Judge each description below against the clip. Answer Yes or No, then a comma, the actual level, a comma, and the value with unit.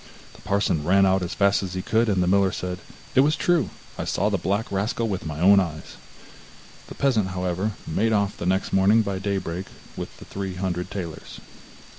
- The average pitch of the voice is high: No, very low, 95 Hz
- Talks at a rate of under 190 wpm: No, average, 195 wpm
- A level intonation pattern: Yes, narrow, 2.0 semitones